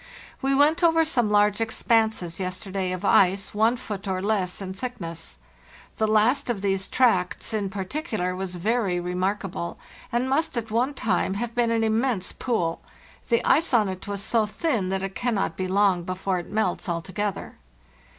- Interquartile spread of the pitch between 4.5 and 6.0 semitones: No, average, 4.0 semitones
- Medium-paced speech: Yes, average, 170 wpm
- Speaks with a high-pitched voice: Yes, high, 205 Hz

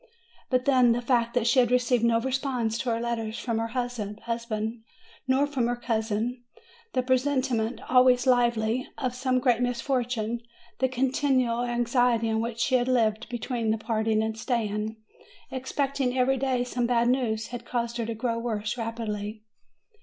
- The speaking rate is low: No, average, 165 wpm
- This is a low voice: No, high, 240 Hz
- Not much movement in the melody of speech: Yes, narrow, 1.9 semitones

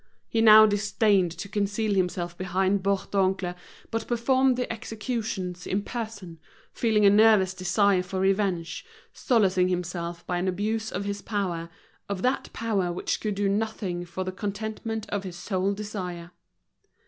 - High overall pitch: Yes, high, 200 Hz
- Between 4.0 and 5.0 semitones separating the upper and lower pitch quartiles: No, average, 2.9 semitones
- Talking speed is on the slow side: No, average, 150 wpm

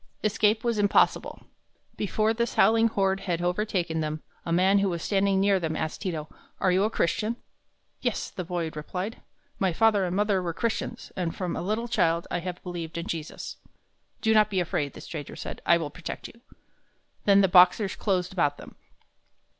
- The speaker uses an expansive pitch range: No, average, 3.7 semitones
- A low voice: No, medium, 185 Hz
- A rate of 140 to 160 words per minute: No, average, 185 wpm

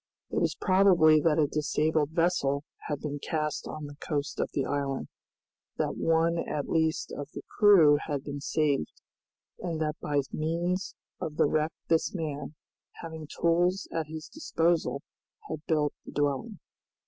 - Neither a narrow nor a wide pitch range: No, narrow, 2.2 semitones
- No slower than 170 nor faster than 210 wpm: No, average, 155 wpm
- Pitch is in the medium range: Yes, medium, 155 Hz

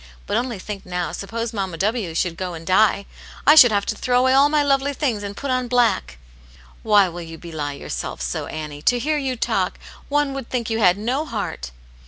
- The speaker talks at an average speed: No, fast, 220 wpm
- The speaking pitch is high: Yes, high, 215 Hz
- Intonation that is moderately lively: No, wide, 6.5 semitones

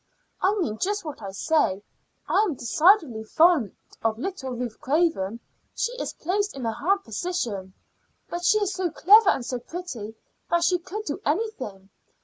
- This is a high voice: Yes, very high, 315 Hz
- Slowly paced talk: No, average, 165 wpm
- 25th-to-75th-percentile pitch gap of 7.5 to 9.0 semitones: Yes, wide, 8.6 semitones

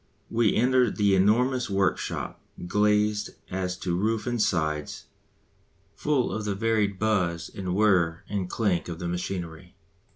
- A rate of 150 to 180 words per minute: No, slow, 135 wpm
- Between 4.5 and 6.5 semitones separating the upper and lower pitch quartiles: No, average, 3.4 semitones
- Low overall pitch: Yes, low, 100 Hz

